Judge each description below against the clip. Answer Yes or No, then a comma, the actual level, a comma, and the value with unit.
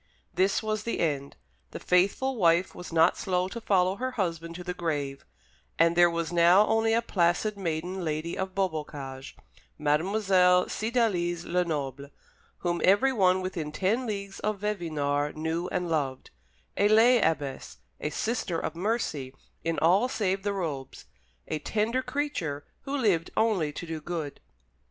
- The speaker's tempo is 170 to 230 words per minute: No, average, 150 wpm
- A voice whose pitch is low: No, medium, 180 Hz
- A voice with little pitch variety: No, average, 4.3 semitones